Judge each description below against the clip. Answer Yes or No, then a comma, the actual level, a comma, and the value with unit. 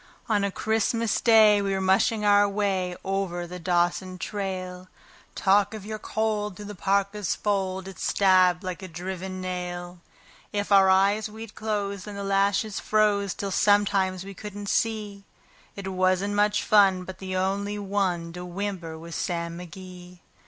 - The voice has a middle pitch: No, high, 195 Hz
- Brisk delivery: No, average, 160 wpm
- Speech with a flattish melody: Yes, narrow, 1.9 semitones